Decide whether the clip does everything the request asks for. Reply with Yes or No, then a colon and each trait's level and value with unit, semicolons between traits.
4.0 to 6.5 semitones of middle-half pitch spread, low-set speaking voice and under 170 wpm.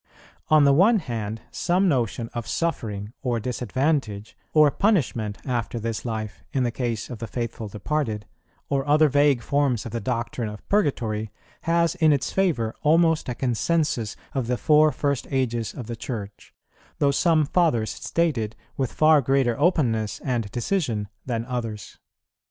Yes: average, 5.1 semitones; low, 125 Hz; average, 155 wpm